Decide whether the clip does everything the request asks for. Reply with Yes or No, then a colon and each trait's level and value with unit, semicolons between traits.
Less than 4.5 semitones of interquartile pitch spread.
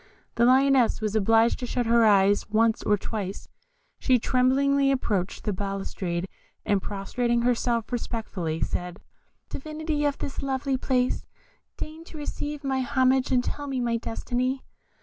Yes: average, 4.1 semitones